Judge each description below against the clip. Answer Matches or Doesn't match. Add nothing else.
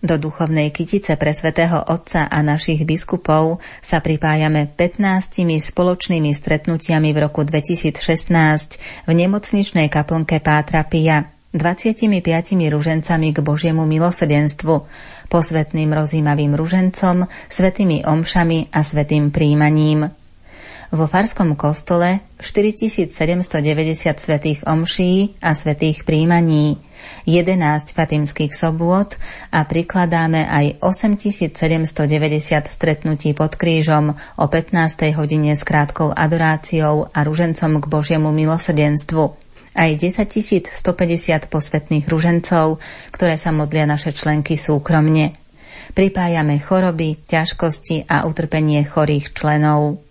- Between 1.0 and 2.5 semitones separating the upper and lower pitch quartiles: Matches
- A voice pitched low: Doesn't match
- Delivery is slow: Matches